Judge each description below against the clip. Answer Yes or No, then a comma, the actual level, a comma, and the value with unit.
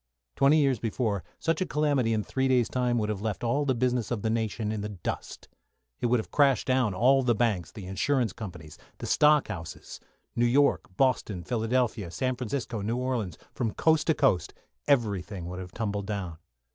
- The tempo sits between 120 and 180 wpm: No, average, 190 wpm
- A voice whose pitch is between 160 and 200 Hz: No, low, 115 Hz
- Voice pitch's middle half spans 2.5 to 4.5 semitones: Yes, average, 4.2 semitones